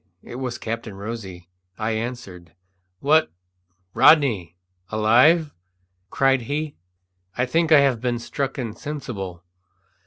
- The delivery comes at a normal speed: No, slow, 105 wpm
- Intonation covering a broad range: No, average, 4.5 semitones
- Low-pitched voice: Yes, low, 120 Hz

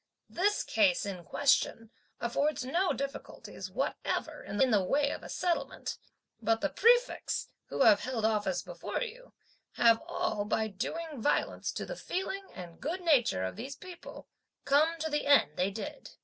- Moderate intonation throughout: No, wide, 7.4 semitones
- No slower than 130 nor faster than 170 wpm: Yes, average, 160 wpm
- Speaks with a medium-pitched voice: No, very high, 275 Hz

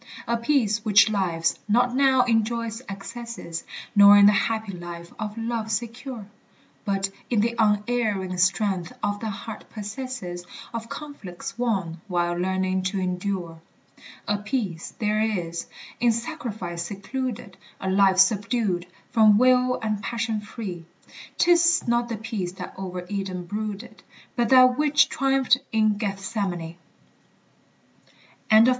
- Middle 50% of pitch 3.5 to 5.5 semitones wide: Yes, average, 3.9 semitones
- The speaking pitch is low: No, high, 210 Hz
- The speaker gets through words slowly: Yes, slow, 130 wpm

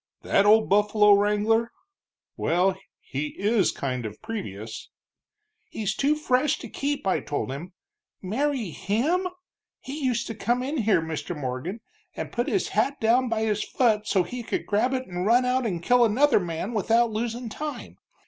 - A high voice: Yes, high, 220 Hz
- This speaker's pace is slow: No, average, 165 wpm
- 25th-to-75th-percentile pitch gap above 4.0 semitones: Yes, average, 4.9 semitones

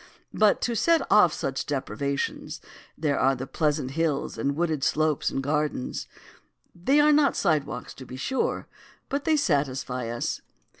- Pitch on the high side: No, medium, 150 Hz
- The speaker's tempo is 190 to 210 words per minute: No, average, 145 wpm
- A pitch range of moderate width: No, wide, 6.5 semitones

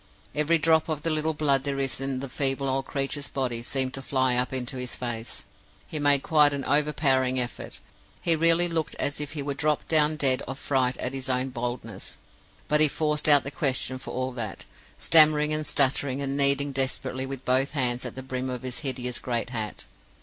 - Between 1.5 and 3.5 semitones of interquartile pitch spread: Yes, narrow, 2.5 semitones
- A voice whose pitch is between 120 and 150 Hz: Yes, low, 135 Hz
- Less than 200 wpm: No, fast, 205 wpm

